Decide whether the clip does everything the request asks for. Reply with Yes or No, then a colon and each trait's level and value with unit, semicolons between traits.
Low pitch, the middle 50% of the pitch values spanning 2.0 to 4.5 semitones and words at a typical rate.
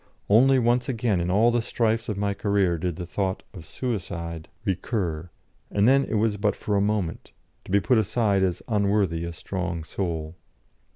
Yes: low, 100 Hz; average, 3.9 semitones; average, 180 wpm